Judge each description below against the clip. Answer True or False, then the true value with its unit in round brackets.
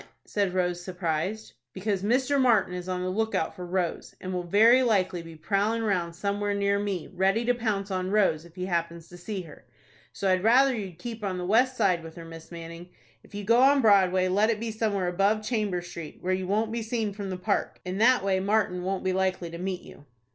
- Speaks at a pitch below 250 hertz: True (190 Hz)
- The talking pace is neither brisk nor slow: False (225 wpm)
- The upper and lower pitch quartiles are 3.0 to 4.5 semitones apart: True (3.3 semitones)